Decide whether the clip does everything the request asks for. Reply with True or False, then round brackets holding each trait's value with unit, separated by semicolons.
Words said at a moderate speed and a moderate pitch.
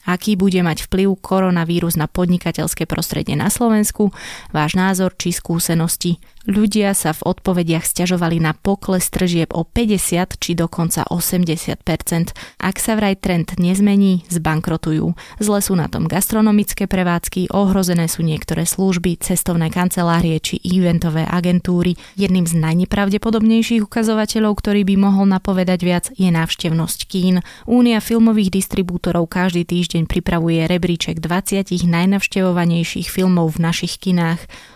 True (125 wpm; 180 Hz)